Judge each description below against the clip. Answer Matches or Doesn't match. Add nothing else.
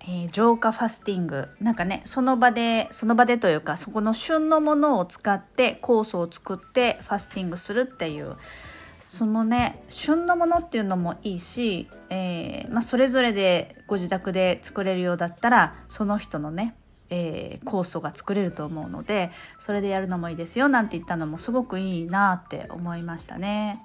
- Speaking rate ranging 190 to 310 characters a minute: Doesn't match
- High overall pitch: Matches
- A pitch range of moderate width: Matches